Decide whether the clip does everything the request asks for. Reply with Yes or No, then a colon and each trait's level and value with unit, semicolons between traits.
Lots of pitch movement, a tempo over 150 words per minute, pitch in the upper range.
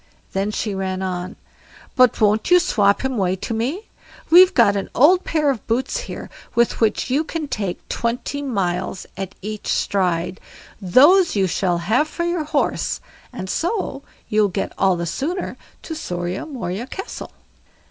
Yes: wide, 7.8 semitones; average, 160 wpm; high, 220 Hz